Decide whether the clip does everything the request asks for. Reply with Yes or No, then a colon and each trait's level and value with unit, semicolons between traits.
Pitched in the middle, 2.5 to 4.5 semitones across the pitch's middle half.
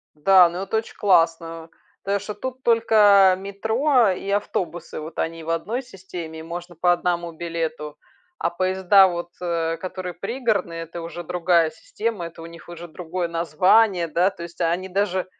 Yes: medium, 175 Hz; average, 2.9 semitones